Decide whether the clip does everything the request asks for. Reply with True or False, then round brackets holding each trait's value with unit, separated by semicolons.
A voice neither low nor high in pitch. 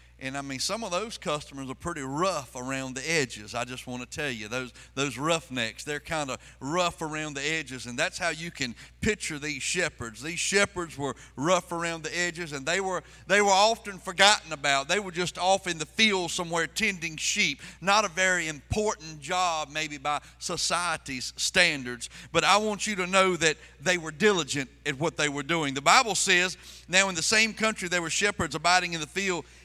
True (165 Hz)